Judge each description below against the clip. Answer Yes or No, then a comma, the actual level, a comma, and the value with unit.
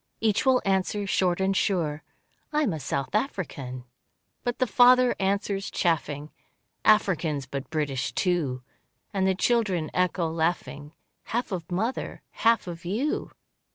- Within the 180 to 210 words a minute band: No, slow, 135 wpm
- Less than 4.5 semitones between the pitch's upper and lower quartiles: No, wide, 5.4 semitones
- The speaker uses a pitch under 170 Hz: No, medium, 185 Hz